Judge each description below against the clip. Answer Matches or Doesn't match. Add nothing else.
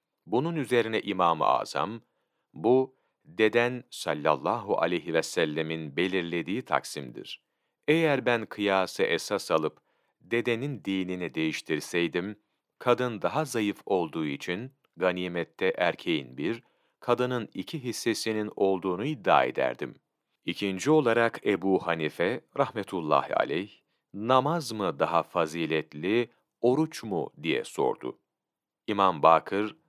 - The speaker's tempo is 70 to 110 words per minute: Matches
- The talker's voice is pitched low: Matches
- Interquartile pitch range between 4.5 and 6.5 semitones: Matches